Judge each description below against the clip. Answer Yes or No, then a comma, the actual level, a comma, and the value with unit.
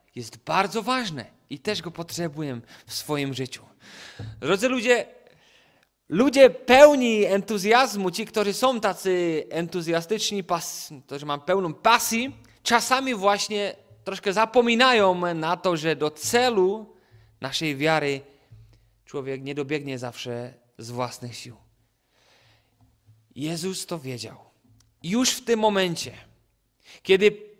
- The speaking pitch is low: No, medium, 165 Hz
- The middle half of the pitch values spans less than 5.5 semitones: No, wide, 9.0 semitones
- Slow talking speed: Yes, slow, 110 wpm